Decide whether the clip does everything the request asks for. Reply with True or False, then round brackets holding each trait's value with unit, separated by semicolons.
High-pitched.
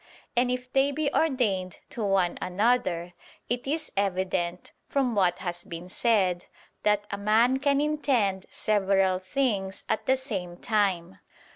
True (205 Hz)